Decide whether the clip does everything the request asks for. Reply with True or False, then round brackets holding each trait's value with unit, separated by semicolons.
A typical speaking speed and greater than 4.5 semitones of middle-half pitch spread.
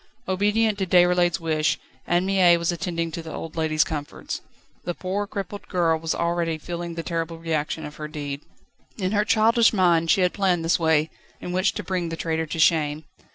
False (195 wpm; 2.4 semitones)